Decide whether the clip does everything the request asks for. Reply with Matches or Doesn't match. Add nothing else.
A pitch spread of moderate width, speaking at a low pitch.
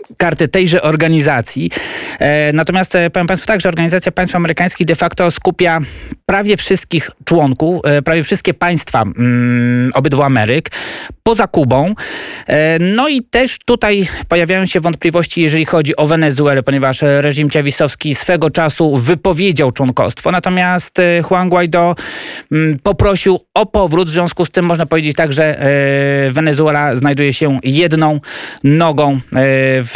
Doesn't match